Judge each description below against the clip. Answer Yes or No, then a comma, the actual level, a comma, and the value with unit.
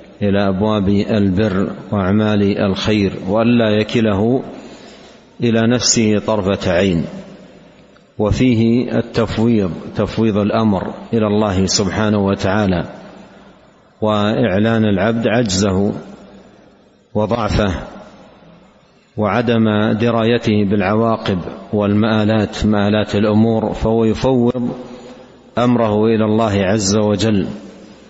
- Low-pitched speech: Yes, low, 105 Hz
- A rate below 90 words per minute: Yes, average, 75 wpm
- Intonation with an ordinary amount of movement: No, narrow, 1.7 semitones